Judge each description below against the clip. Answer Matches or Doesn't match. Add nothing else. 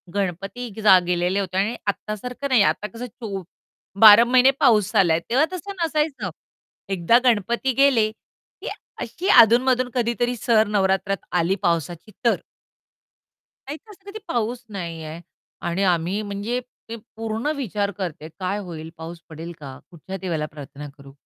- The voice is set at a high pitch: Matches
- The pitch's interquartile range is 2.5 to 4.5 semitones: Doesn't match